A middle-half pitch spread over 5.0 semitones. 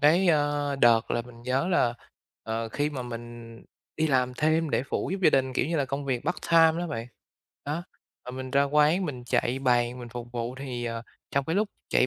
No: average, 3.8 semitones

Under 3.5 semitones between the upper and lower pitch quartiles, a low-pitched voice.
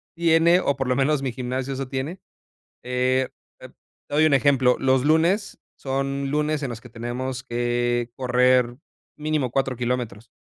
Yes: narrow, 2.4 semitones; low, 130 Hz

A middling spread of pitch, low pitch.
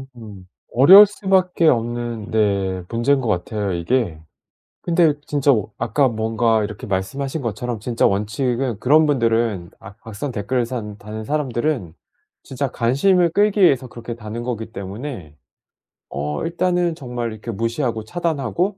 Yes: average, 4.9 semitones; low, 120 Hz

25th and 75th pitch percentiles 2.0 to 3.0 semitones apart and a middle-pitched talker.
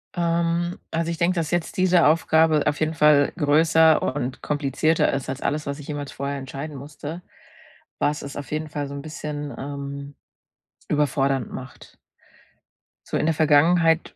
Yes: narrow, 2.4 semitones; medium, 150 Hz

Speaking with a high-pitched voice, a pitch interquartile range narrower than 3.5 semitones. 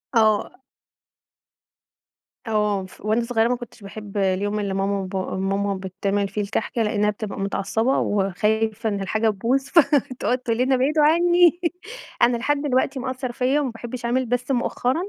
No: high, 225 Hz; average, 4.0 semitones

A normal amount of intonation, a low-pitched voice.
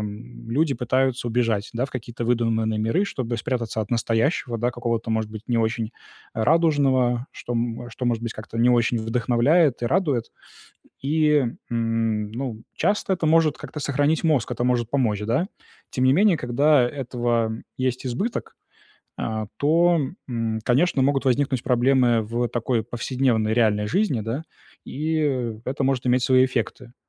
Yes: average, 3.1 semitones; low, 120 Hz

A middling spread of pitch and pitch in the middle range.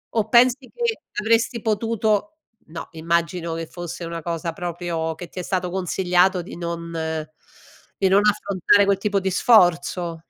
Yes: average, 3.7 semitones; medium, 180 Hz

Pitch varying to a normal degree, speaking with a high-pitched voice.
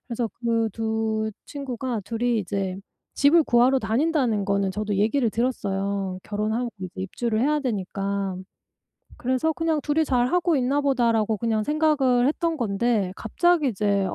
Yes: average, 4.9 semitones; high, 235 Hz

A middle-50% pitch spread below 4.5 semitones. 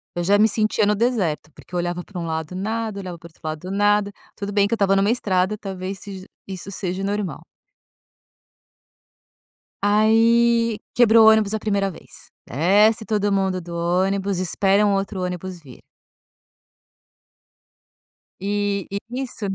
Yes: narrow, 2.5 semitones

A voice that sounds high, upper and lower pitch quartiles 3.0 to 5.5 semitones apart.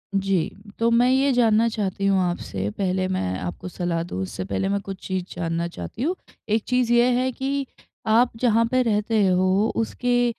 Yes: high, 210 Hz; average, 4.7 semitones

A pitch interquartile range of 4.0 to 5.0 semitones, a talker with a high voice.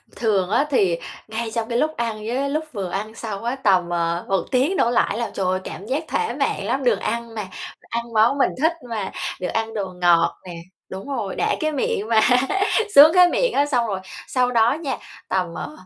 No: wide, 5.4 semitones; high, 230 Hz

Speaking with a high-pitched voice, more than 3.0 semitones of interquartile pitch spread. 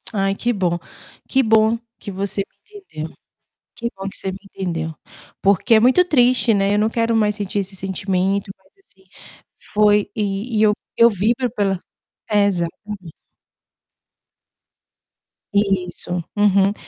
No: high, 200 Hz; narrow, 2.5 semitones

